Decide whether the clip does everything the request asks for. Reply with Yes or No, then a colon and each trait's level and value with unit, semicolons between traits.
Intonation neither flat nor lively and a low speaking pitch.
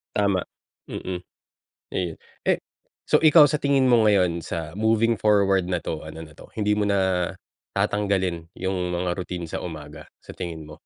Yes: average, 3.5 semitones; very low, 95 Hz